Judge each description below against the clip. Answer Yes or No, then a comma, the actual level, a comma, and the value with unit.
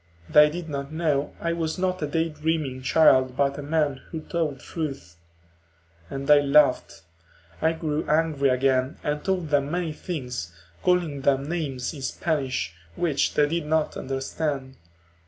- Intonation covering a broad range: No, average, 2.9 semitones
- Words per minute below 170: Yes, average, 150 wpm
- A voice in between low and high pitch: Yes, medium, 150 Hz